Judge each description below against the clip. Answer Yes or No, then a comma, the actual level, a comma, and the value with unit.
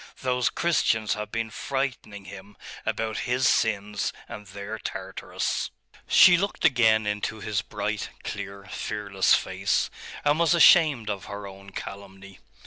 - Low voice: Yes, low, 105 Hz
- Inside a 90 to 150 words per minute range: Yes, slow, 135 wpm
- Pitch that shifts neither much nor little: Yes, average, 4.0 semitones